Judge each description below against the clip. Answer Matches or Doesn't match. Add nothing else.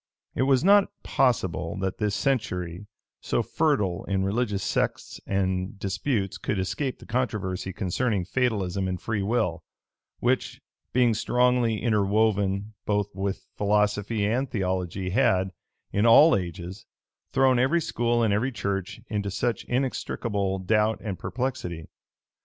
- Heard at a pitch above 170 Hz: Doesn't match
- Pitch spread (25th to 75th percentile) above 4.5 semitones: Doesn't match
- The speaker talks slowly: Matches